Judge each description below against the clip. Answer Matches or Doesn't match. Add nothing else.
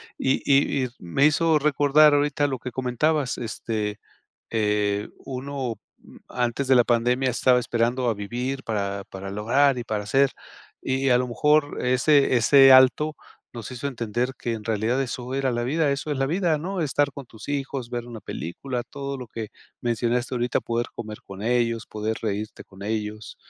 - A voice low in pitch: Matches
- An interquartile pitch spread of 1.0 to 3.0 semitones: Doesn't match